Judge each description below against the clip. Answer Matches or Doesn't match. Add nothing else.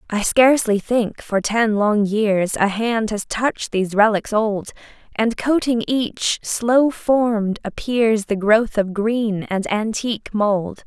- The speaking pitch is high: Matches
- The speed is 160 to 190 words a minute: Doesn't match